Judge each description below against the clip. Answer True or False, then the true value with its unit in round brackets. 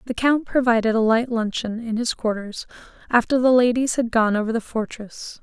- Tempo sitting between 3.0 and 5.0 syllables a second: False (5.2 syllables/s)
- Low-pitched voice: False (230 Hz)